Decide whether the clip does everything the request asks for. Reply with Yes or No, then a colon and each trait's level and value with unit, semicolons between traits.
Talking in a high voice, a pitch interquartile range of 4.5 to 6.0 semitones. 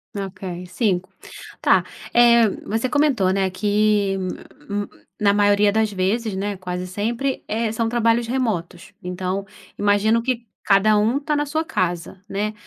No: high, 210 Hz; average, 3.2 semitones